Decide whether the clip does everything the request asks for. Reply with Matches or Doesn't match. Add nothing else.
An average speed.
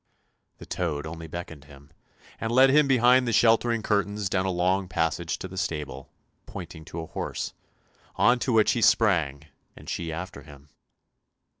Matches